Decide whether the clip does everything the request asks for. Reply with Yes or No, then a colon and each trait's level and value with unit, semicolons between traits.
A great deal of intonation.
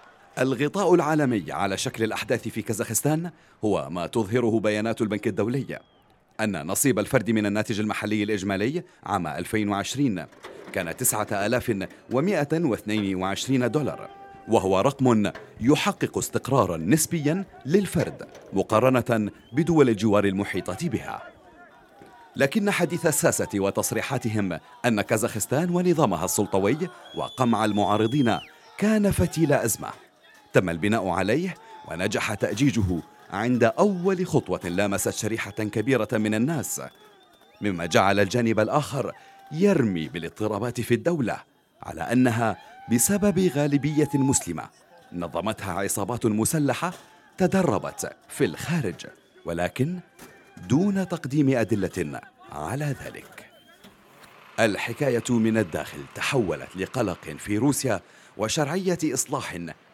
Yes: wide, 6.1 semitones